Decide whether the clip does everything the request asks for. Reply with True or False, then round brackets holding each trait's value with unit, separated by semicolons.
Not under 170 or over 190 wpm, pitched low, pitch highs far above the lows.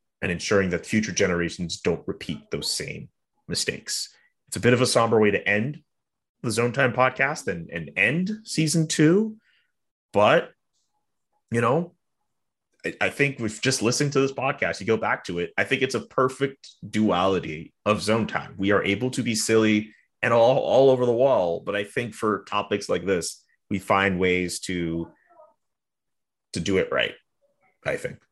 True (175 wpm; 120 Hz; 6.8 semitones)